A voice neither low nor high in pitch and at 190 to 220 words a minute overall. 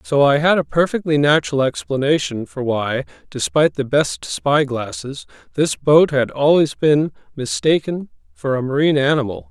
No: medium, 145 Hz; average, 145 wpm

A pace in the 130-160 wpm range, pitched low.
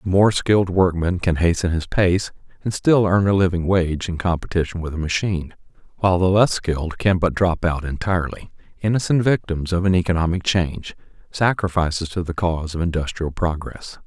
No: average, 175 wpm; very low, 90 Hz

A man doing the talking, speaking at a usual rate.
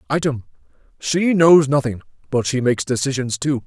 No: male; slow, 130 wpm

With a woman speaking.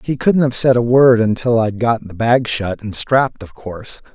No: male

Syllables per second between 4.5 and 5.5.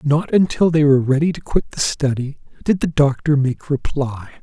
Yes: 5.0 syllables/s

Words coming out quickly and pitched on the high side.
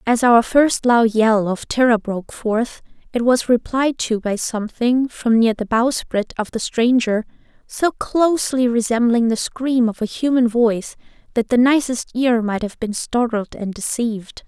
No: average, 170 wpm; high, 235 Hz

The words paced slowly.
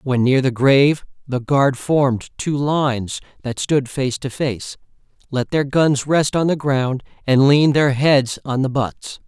No: average, 180 wpm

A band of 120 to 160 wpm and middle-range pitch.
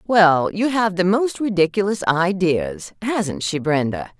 Yes: average, 145 wpm; medium, 180 Hz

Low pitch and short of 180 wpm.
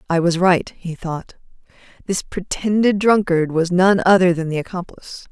No: medium, 180 Hz; average, 160 wpm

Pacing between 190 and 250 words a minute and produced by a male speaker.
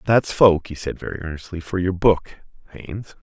No: average, 180 wpm; male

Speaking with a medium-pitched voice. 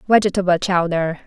Yes: medium, 180 Hz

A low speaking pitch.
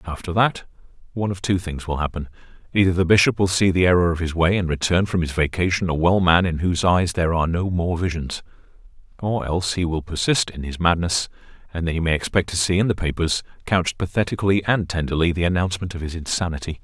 Yes: very low, 90 Hz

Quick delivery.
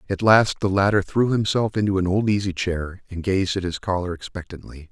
Yes: fast, 210 wpm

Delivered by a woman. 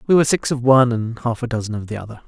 No: male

